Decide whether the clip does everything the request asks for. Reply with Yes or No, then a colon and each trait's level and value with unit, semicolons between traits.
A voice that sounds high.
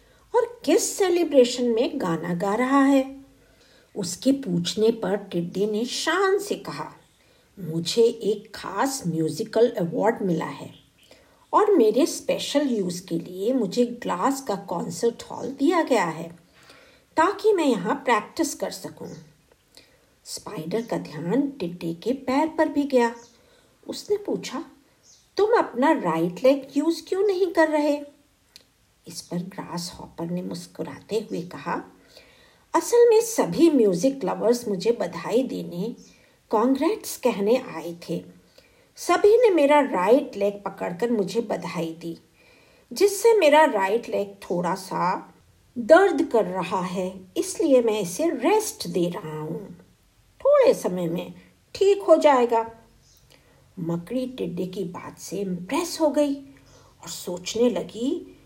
Yes: high, 235 Hz